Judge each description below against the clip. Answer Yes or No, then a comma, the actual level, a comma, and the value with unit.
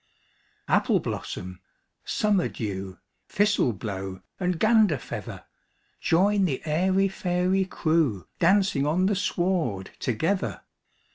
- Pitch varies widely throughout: Yes, wide, 8.3 semitones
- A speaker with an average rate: No, slow, 65 wpm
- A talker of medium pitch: Yes, medium, 175 Hz